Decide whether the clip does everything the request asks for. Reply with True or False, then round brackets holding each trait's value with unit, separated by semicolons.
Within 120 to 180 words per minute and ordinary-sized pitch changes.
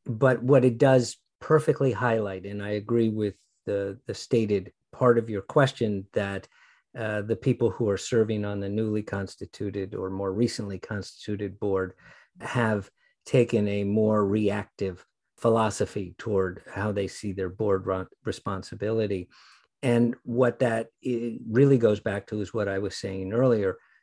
True (150 wpm; 3.2 semitones)